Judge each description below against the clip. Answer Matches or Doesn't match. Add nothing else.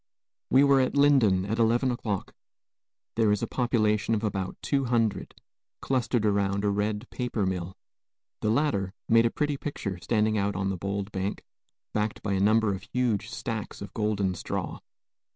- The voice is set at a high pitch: Doesn't match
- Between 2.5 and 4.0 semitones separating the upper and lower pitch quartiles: Matches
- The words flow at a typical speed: Matches